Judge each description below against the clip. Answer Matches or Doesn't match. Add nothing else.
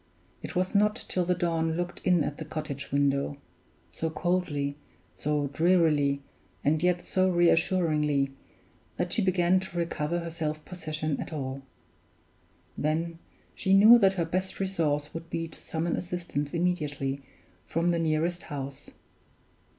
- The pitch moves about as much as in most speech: Matches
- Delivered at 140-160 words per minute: Matches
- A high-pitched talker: Doesn't match